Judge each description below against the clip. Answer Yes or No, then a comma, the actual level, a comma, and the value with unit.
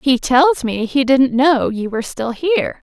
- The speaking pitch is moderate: No, very high, 265 Hz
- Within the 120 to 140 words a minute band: No, fast, 205 wpm